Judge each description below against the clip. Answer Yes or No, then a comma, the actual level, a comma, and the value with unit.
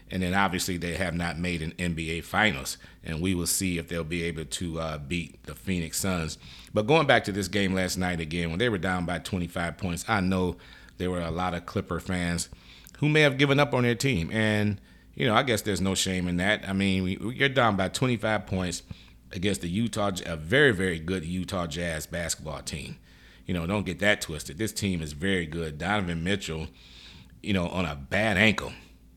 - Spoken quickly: Yes, fast, 215 wpm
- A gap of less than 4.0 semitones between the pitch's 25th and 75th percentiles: Yes, average, 3.0 semitones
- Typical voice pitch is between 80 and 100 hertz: Yes, very low, 90 Hz